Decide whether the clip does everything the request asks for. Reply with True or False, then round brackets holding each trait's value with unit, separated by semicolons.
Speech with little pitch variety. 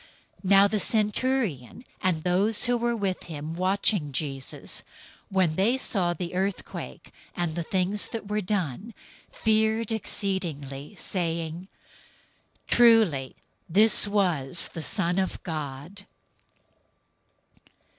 False (4.5 semitones)